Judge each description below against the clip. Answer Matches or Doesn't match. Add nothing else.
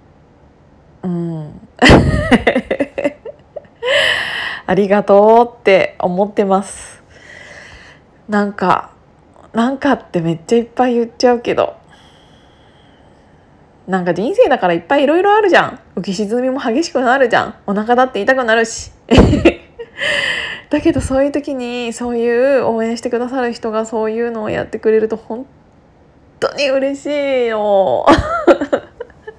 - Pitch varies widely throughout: Doesn't match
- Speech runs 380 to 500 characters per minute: Doesn't match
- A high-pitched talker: Matches